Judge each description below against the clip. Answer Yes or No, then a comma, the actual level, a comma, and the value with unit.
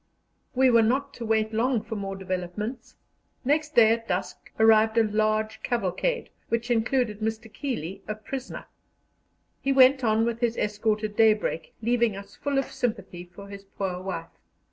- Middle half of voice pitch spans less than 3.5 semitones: Yes, average, 3.0 semitones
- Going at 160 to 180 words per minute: Yes, average, 165 wpm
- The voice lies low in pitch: No, high, 220 Hz